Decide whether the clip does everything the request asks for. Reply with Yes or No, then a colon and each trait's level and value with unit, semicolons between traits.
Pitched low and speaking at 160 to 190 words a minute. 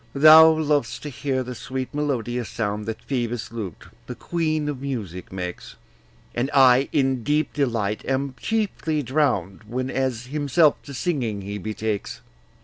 No: low, 130 Hz; average, 140 wpm